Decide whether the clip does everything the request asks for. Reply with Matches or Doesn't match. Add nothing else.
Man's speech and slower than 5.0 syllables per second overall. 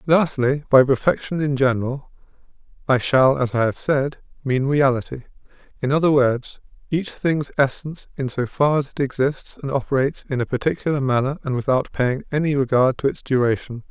Doesn't match